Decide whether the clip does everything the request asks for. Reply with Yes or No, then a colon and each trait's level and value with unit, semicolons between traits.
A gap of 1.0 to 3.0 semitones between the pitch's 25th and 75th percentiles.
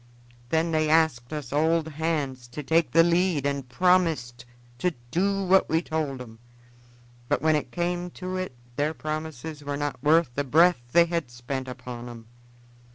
No: average, 4.2 semitones